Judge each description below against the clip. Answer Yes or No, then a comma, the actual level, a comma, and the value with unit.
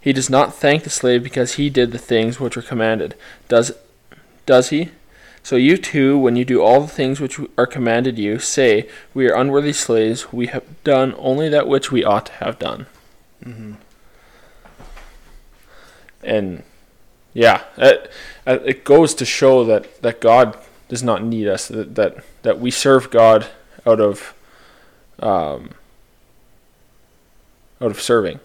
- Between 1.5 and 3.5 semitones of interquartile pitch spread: Yes, average, 3.2 semitones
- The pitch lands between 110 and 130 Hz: Yes, low, 125 Hz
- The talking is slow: No, average, 155 wpm